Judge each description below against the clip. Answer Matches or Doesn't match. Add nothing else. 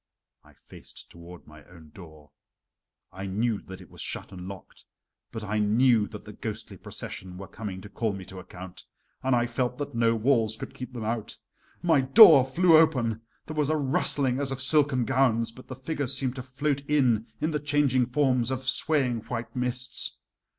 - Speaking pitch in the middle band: Doesn't match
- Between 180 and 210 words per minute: Matches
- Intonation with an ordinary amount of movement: Matches